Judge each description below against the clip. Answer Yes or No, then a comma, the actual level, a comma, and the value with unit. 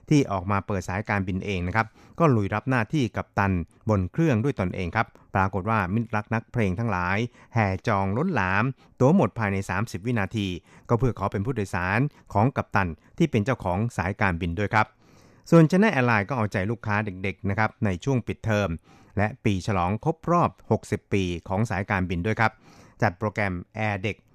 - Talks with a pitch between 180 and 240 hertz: No, low, 105 Hz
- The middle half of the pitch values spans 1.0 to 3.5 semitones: Yes, average, 3.2 semitones